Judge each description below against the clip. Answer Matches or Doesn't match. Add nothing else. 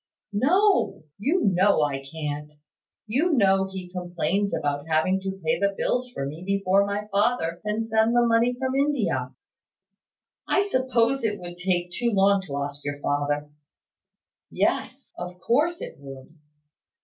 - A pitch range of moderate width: Doesn't match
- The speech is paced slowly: Doesn't match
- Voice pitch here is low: Doesn't match